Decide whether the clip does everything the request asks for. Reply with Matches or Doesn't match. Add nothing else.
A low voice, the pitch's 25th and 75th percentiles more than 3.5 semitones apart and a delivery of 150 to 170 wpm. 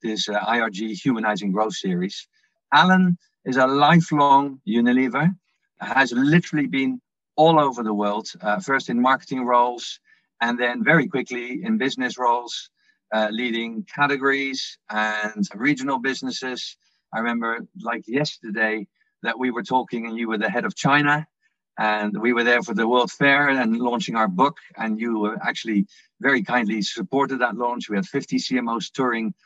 Matches